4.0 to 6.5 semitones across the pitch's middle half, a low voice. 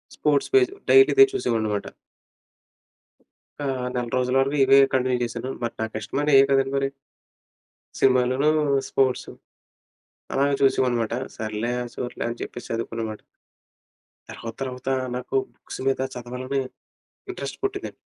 No: narrow, 2.5 semitones; low, 130 Hz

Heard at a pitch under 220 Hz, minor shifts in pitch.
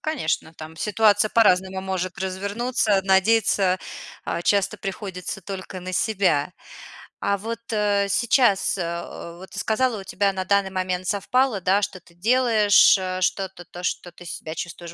Yes: high, 190 Hz; narrow, 2.3 semitones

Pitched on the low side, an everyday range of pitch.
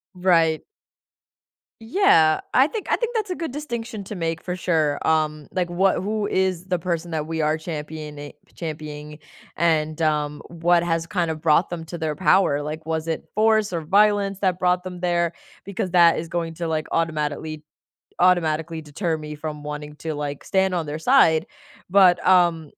No: medium, 165 Hz; average, 3.0 semitones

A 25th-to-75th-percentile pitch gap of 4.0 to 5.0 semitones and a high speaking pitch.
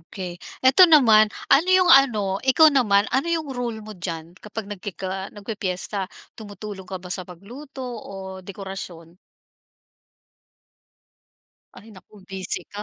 Yes: average, 4.7 semitones; high, 205 Hz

